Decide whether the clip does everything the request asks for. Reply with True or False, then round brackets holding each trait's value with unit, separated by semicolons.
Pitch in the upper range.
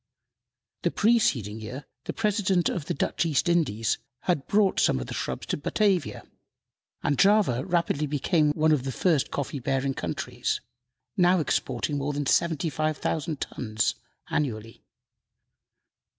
False (150 Hz)